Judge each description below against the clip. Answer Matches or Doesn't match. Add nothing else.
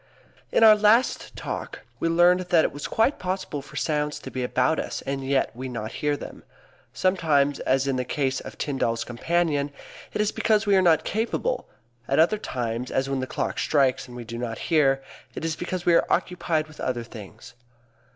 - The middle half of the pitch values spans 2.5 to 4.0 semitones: Doesn't match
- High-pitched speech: Doesn't match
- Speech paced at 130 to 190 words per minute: Doesn't match